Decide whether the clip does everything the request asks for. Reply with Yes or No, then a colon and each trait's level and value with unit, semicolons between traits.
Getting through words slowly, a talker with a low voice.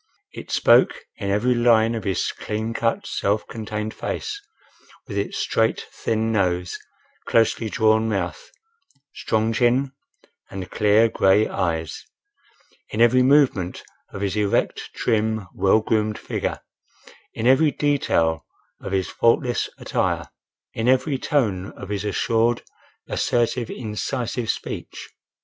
Yes: slow, 125 wpm; low, 110 Hz